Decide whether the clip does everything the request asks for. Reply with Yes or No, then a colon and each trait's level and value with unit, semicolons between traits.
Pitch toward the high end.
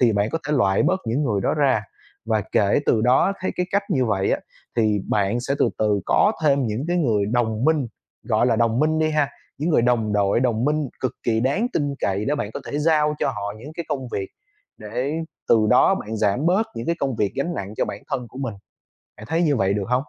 No: low, 125 Hz